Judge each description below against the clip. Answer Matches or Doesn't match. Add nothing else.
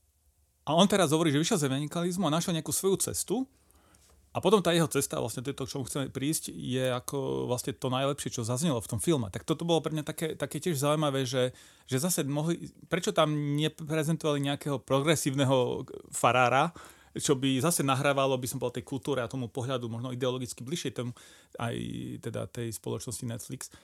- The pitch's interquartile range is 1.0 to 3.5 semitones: Doesn't match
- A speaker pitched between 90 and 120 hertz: Doesn't match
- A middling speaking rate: Doesn't match